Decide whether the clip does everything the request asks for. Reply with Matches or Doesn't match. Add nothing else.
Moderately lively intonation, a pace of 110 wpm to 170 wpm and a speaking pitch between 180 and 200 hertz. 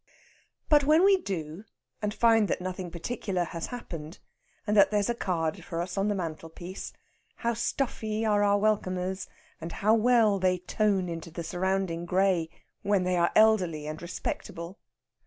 Matches